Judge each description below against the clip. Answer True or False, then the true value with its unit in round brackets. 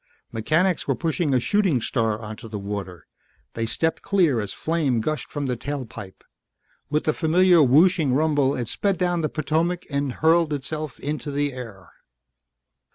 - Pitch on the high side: False (145 Hz)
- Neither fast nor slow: True (160 wpm)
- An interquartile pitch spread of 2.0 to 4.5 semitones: False (5.3 semitones)